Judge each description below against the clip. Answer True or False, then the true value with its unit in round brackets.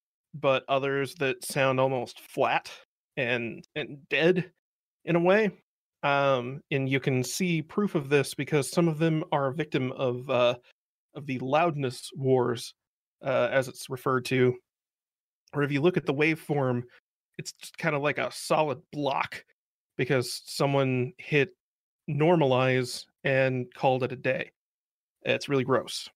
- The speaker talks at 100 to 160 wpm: True (150 wpm)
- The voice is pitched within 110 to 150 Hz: True (135 Hz)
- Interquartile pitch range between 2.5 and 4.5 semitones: True (3.1 semitones)